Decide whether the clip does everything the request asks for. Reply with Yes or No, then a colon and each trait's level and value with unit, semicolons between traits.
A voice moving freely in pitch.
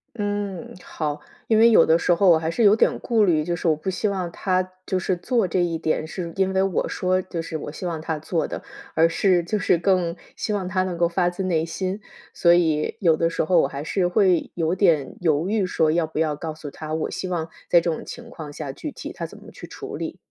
No: average, 2.9 semitones